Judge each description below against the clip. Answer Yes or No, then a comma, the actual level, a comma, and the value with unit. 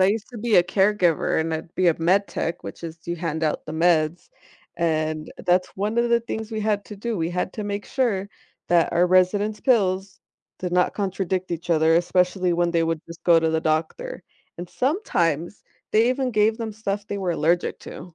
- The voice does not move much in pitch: No, average, 3.8 semitones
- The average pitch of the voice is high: No, medium, 180 Hz